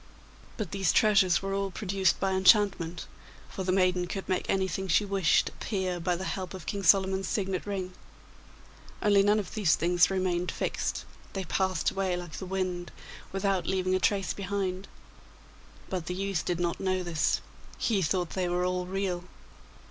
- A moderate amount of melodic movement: No, narrow, 1.5 semitones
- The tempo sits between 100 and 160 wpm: No, average, 170 wpm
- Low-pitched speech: No, high, 190 Hz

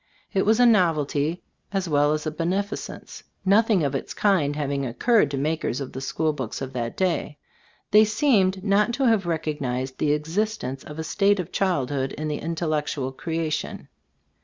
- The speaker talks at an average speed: Yes, average, 180 wpm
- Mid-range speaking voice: Yes, medium, 160 Hz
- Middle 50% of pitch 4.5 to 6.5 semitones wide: Yes, wide, 5.4 semitones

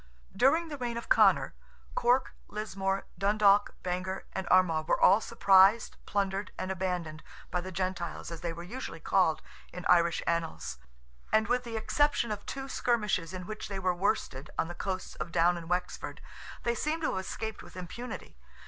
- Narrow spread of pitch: No, average, 3.8 semitones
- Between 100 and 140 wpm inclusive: No, average, 175 wpm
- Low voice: No, high, 190 Hz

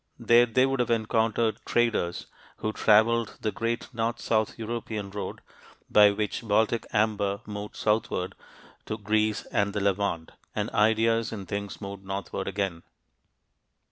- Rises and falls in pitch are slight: Yes, narrow, 2.1 semitones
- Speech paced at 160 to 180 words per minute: No, average, 140 wpm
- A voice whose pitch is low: Yes, low, 110 Hz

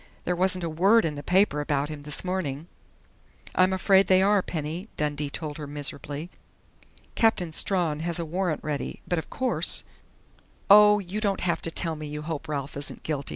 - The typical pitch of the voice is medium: Yes, medium, 165 Hz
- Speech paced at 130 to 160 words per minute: No, average, 195 wpm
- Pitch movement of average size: Yes, average, 3.9 semitones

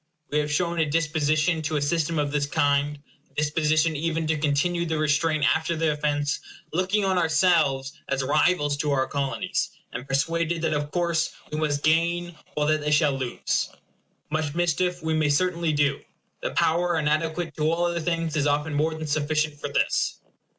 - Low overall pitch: No, medium, 155 Hz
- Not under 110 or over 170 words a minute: No, average, 180 wpm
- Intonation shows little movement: Yes, narrow, 2.2 semitones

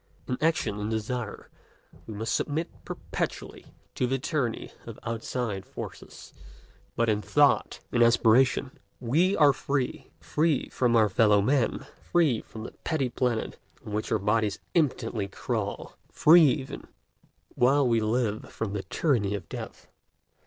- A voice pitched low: Yes, low, 120 Hz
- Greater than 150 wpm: No, average, 140 wpm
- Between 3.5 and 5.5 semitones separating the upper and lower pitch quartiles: Yes, average, 4.2 semitones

